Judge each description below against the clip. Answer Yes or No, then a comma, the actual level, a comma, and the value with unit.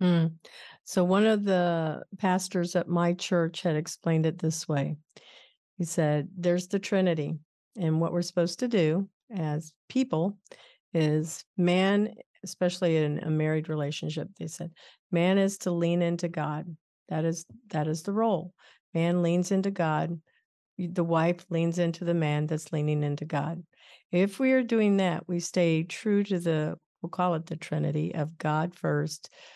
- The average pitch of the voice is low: No, medium, 170 Hz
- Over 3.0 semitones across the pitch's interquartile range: No, average, 2.7 semitones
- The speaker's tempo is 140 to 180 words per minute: Yes, average, 160 wpm